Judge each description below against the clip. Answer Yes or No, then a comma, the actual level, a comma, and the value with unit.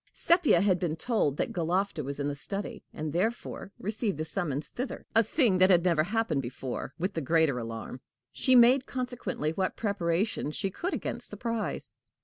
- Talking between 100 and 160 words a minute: No, average, 175 wpm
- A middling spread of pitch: No, wide, 6.5 semitones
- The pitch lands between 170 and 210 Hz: Yes, medium, 185 Hz